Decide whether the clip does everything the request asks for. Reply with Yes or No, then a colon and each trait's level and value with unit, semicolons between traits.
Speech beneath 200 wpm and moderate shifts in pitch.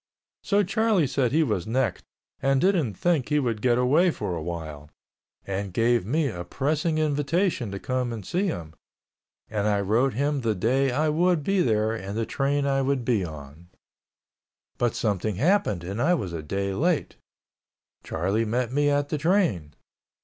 No: average, 170 wpm; wide, 6.9 semitones